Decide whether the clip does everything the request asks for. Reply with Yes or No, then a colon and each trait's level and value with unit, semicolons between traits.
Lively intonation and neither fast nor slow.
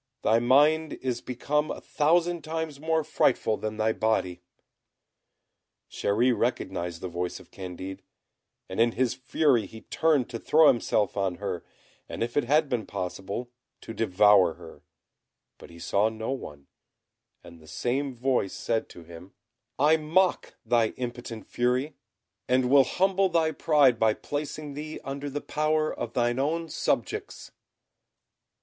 Yes: wide, 5.9 semitones; average, 145 wpm